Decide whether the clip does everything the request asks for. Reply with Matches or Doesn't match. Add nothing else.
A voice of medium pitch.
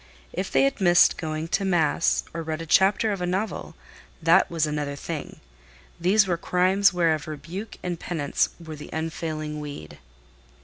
Matches